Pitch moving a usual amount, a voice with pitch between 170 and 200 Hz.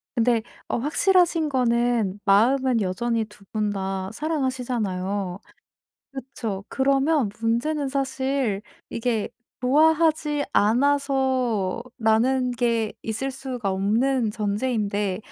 No: average, 4.3 semitones; high, 240 Hz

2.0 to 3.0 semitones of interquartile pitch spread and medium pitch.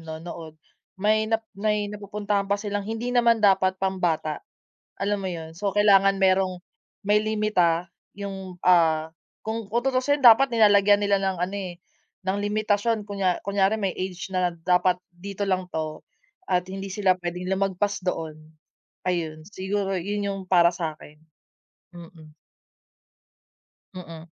No: narrow, 2.6 semitones; high, 195 Hz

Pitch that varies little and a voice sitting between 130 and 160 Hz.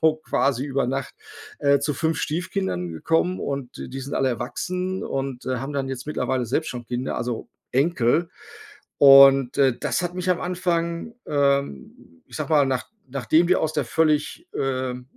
No: average, 4.1 semitones; medium, 140 Hz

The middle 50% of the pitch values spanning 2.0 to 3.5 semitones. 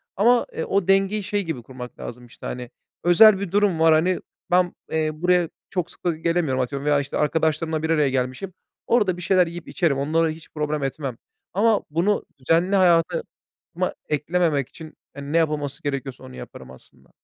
No: average, 4.2 semitones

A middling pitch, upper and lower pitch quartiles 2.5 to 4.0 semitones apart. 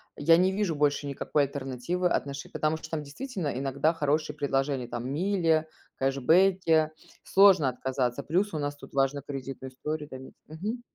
Yes: medium, 150 Hz; average, 3.5 semitones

